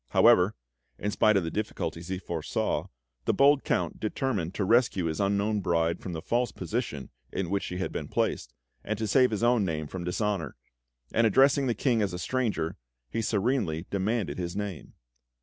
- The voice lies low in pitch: Yes, low, 100 Hz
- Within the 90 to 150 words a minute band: No, average, 185 wpm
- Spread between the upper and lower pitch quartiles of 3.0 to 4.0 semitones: No, average, 4.7 semitones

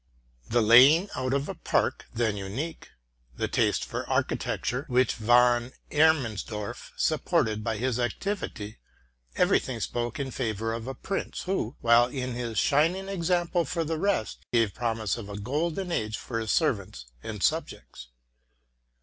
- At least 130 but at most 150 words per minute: No, average, 160 wpm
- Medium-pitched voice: No, low, 120 Hz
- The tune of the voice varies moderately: No, wide, 6.0 semitones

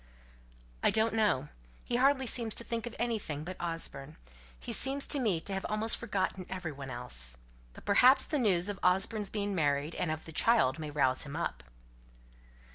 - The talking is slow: No, average, 185 wpm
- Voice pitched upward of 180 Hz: Yes, high, 190 Hz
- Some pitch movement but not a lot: No, wide, 7.1 semitones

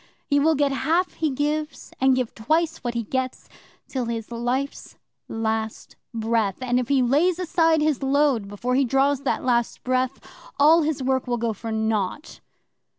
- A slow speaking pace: No, average, 170 wpm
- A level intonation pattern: No, average, 3.9 semitones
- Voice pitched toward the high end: Yes, very high, 260 Hz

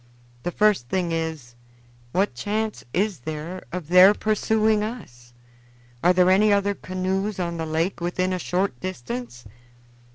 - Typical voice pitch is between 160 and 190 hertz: Yes, medium, 185 Hz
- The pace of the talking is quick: No, average, 140 wpm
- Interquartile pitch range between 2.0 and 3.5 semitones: No, average, 3.9 semitones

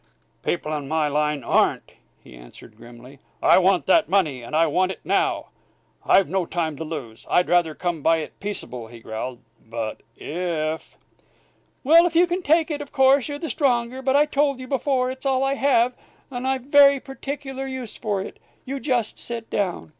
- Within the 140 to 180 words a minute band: No, average, 190 wpm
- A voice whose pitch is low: No, high, 210 Hz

